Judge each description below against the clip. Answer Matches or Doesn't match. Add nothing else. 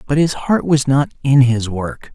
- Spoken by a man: Matches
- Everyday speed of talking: Doesn't match